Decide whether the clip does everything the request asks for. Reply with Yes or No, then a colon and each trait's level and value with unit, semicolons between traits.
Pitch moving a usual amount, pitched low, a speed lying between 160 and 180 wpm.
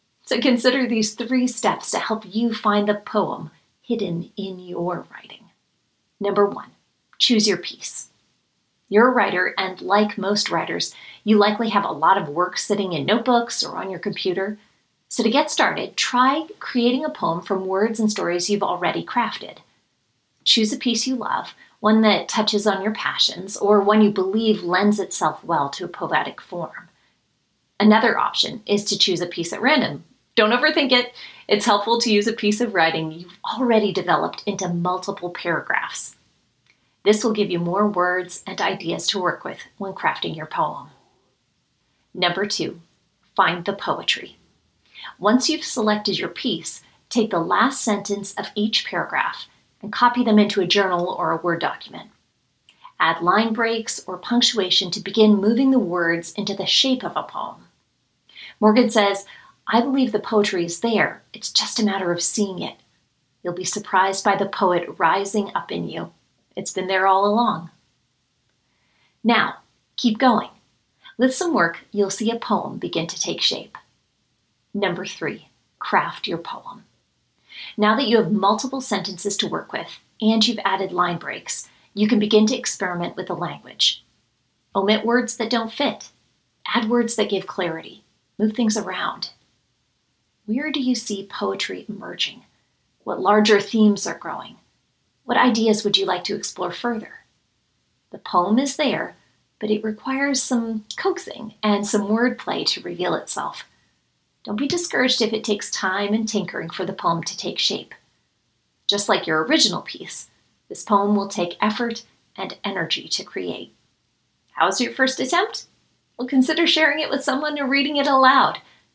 No: average, 3.6 semitones; high, 210 Hz; average, 165 wpm